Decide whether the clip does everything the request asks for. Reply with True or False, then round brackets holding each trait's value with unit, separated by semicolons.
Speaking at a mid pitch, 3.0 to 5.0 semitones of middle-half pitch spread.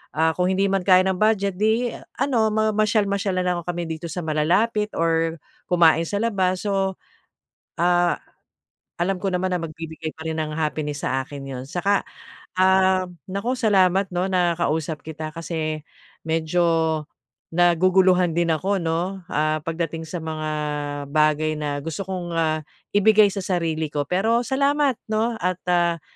True (175 Hz; 3.4 semitones)